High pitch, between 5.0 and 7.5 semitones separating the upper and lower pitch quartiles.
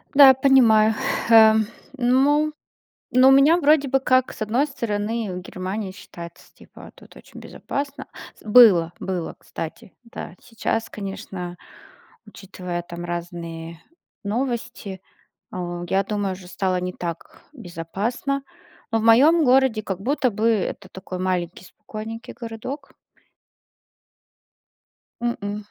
Yes: high, 215 Hz; wide, 5.6 semitones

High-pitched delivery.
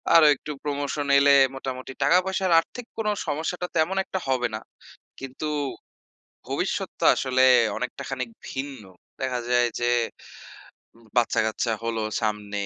No: low, 135 Hz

